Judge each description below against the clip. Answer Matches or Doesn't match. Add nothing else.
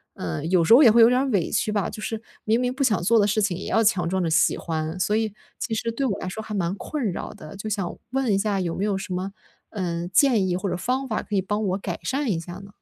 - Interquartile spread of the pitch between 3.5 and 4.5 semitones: Matches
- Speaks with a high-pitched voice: Matches